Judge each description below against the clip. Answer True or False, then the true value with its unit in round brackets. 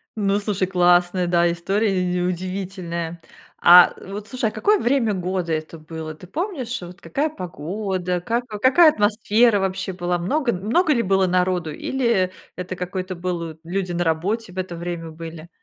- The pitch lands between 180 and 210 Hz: True (185 Hz)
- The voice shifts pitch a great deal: False (3.4 semitones)